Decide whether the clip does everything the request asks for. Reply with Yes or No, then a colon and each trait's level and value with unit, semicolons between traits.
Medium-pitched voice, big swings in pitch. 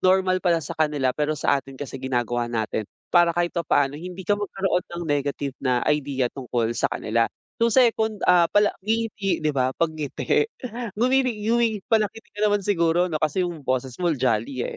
Yes: medium, 165 Hz; wide, 6.9 semitones